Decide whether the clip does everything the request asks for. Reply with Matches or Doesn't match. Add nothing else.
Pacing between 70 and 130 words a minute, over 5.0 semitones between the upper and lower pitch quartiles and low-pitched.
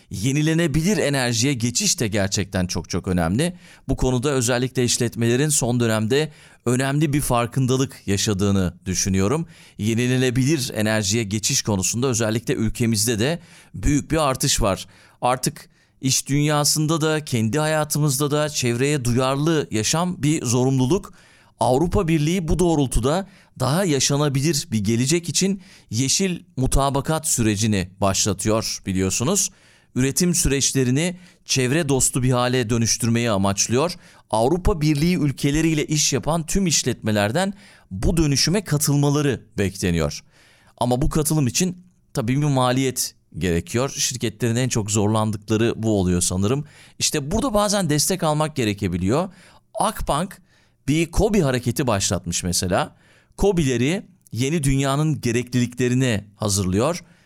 Matches